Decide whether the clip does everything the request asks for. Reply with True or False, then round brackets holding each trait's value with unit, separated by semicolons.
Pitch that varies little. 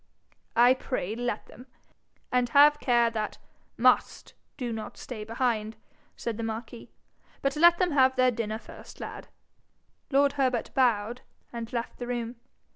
True (2.3 semitones)